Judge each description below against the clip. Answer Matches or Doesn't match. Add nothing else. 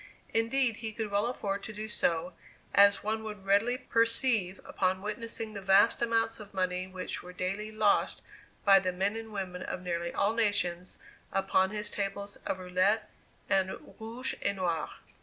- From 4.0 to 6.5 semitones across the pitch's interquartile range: Doesn't match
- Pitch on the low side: Doesn't match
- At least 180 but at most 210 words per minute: Doesn't match